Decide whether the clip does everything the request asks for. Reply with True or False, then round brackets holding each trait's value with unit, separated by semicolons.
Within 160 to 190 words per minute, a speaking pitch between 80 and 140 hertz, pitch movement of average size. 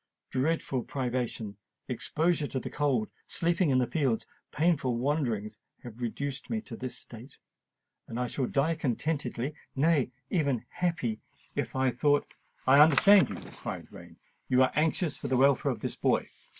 False (145 wpm; 135 Hz; 3.8 semitones)